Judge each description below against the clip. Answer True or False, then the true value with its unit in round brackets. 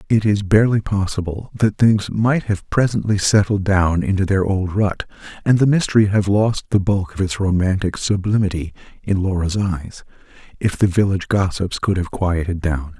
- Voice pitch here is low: True (100 Hz)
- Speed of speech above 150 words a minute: True (170 wpm)